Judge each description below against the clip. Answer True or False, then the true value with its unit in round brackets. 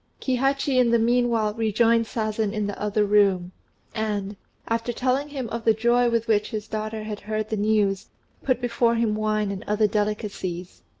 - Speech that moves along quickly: False (175 wpm)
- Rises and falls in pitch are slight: True (2.0 semitones)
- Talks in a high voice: True (220 Hz)